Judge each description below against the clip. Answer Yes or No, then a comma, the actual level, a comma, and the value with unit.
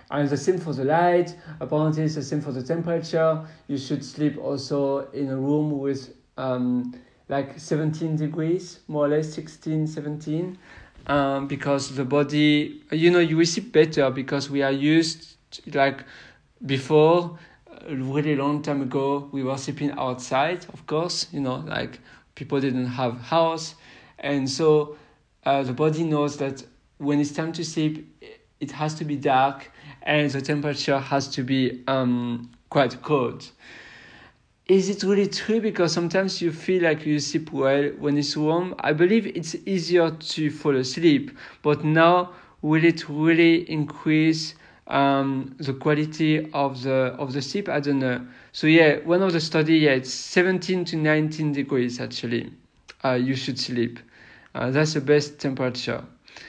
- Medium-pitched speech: Yes, medium, 150 Hz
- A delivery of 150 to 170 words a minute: Yes, average, 160 wpm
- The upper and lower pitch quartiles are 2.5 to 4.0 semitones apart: Yes, average, 2.9 semitones